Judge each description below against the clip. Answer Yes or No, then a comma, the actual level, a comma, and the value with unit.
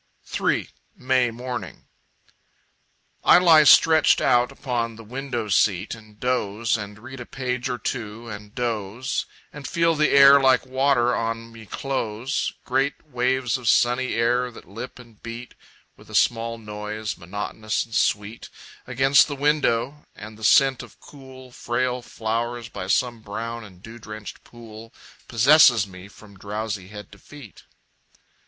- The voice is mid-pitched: No, low, 120 Hz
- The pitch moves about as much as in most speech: Yes, average, 3.3 semitones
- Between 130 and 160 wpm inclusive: Yes, average, 150 wpm